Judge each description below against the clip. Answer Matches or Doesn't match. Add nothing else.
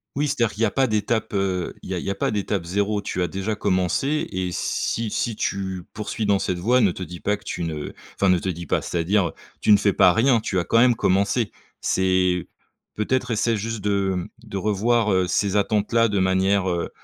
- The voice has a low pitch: Matches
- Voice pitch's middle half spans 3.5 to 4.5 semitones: Doesn't match